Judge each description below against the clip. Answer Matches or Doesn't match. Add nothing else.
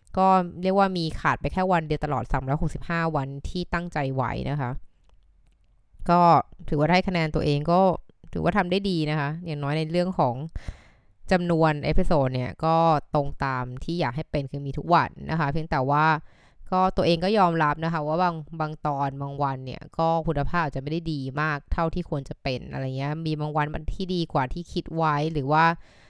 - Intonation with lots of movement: Doesn't match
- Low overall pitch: Doesn't match